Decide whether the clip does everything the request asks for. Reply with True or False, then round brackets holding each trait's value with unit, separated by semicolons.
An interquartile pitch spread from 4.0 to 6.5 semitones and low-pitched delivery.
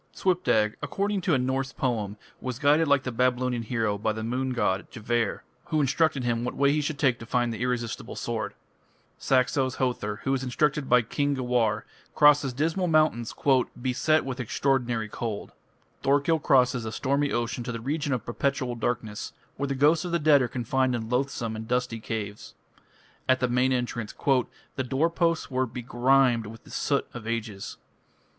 False (3.2 semitones; 125 Hz)